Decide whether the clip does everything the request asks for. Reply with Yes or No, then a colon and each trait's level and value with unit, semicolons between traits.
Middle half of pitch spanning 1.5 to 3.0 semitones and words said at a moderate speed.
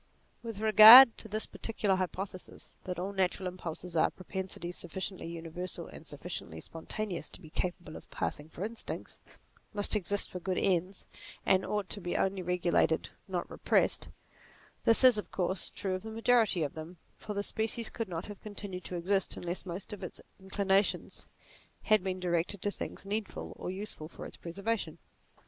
Yes: average, 2.7 semitones; average, 170 wpm